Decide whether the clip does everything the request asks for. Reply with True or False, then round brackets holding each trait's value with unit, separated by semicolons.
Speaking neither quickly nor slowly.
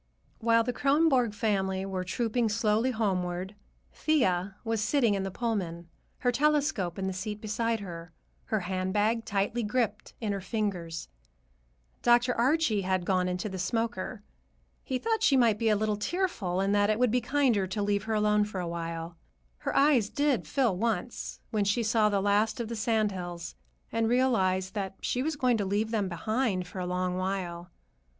True (180 wpm)